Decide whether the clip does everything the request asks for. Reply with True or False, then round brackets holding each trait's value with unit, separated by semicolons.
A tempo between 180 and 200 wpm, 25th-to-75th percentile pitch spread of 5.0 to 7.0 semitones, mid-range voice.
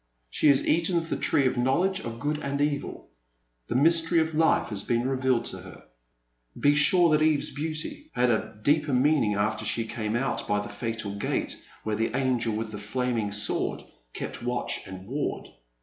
False (190 wpm; 5.4 semitones; 130 Hz)